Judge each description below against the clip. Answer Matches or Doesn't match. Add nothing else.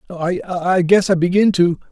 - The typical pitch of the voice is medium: Matches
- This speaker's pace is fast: Doesn't match